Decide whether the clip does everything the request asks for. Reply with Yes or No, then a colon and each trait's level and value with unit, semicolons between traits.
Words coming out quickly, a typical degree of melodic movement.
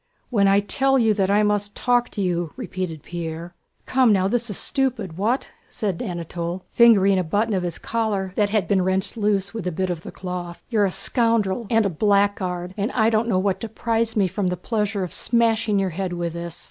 Yes: fast, 210 wpm; average, 3.6 semitones